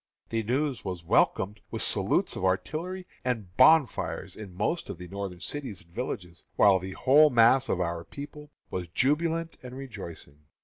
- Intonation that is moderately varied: No, wide, 7.8 semitones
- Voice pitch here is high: No, low, 115 Hz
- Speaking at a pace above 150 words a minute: Yes, average, 165 wpm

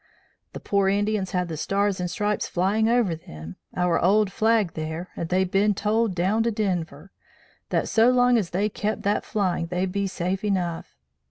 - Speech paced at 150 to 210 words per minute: Yes, average, 180 wpm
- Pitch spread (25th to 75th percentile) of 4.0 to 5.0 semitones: No, average, 2.9 semitones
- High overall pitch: Yes, high, 195 Hz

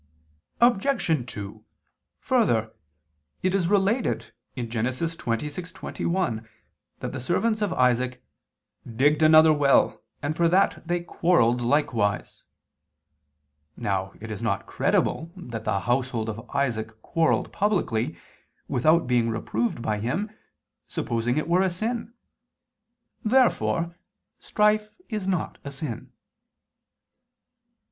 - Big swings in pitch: Yes, wide, 8.0 semitones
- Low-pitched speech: No, medium, 145 Hz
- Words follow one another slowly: Yes, slow, 105 wpm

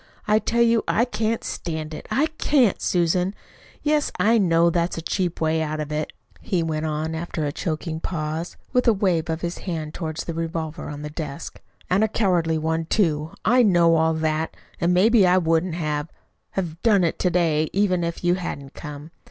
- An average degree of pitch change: Yes, average, 3.0 semitones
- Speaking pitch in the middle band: Yes, medium, 170 Hz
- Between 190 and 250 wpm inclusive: Yes, average, 195 wpm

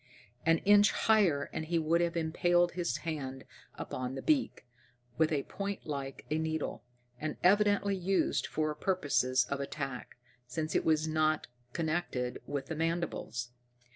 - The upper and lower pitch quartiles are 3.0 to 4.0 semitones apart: Yes, average, 3.7 semitones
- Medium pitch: Yes, medium, 160 Hz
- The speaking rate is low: No, average, 145 wpm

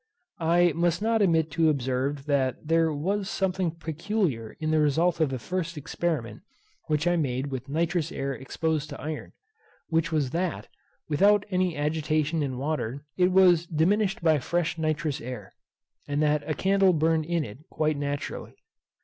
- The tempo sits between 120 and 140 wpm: No, average, 160 wpm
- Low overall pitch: No, medium, 160 Hz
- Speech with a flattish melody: No, average, 3.3 semitones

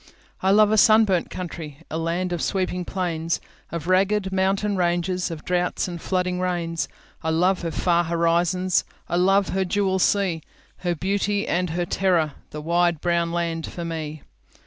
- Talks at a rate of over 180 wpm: No, slow, 135 wpm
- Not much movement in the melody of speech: Yes, narrow, 2.1 semitones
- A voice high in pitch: No, medium, 175 Hz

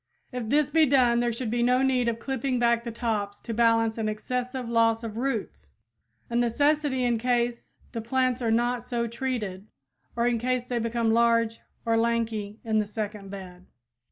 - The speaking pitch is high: Yes, high, 235 Hz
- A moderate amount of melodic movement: No, narrow, 1.7 semitones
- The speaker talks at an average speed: Yes, average, 185 wpm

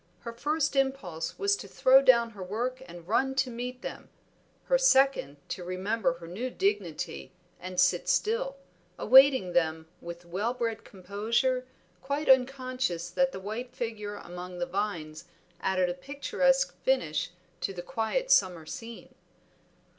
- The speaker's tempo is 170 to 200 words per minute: No, average, 145 wpm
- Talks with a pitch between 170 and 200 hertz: No, high, 225 Hz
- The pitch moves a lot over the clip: Yes, wide, 6.7 semitones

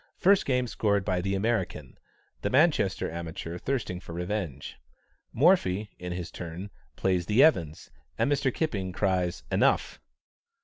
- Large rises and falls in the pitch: No, average, 4.9 semitones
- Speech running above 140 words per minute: No, slow, 135 wpm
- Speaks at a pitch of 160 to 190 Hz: No, very low, 95 Hz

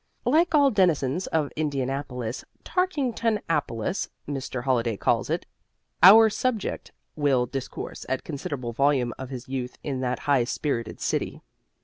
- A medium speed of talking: No, slow, 125 wpm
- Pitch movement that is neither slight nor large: No, wide, 6.9 semitones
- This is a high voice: No, medium, 140 Hz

